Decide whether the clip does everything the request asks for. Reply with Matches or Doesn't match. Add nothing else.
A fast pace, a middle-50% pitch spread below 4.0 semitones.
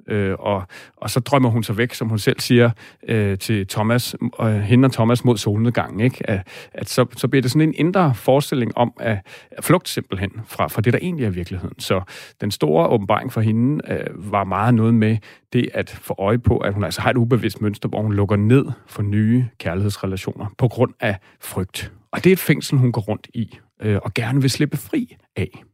Doesn't match